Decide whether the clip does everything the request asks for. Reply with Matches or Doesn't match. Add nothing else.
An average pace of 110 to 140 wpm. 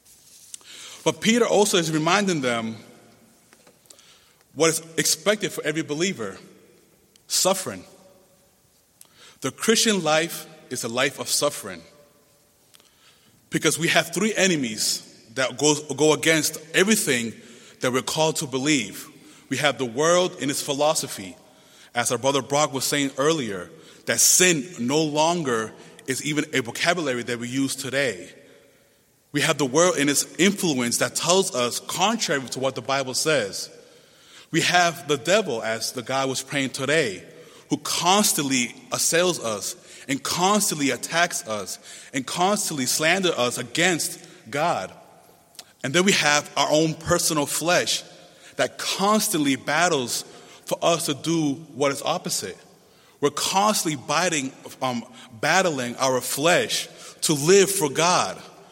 Matches